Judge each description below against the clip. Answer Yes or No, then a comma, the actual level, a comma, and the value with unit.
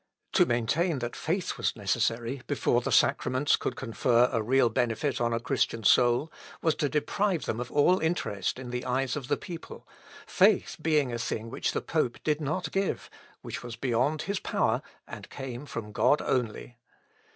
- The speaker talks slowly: No, average, 175 wpm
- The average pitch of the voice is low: Yes, low, 130 Hz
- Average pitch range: Yes, average, 4.2 semitones